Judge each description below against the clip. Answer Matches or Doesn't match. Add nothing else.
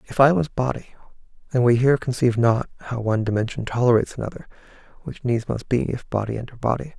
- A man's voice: Matches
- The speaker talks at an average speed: Matches